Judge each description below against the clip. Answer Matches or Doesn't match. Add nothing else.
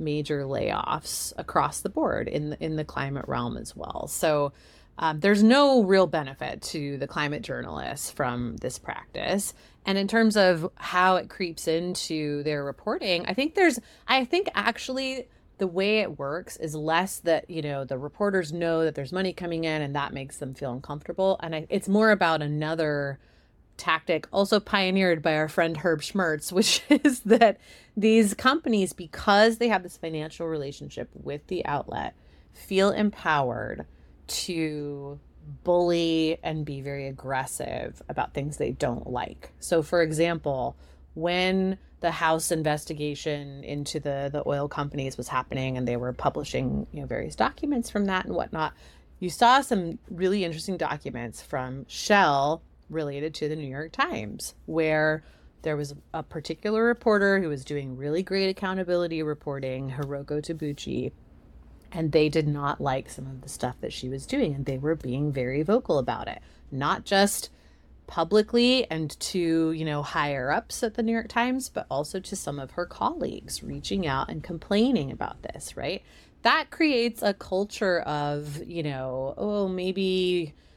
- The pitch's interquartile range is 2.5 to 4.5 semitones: Doesn't match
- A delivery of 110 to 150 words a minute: Doesn't match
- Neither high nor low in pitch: Matches